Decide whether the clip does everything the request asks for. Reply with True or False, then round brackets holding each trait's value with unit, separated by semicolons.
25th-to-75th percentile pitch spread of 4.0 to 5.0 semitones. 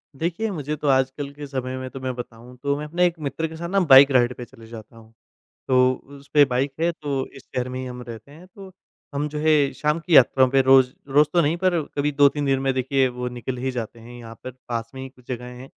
False (2.9 semitones)